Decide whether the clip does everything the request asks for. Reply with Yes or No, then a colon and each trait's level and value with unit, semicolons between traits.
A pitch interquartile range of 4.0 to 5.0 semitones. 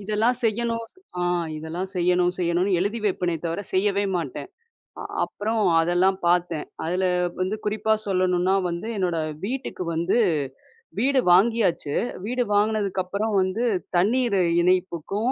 No: average, 3.5 semitones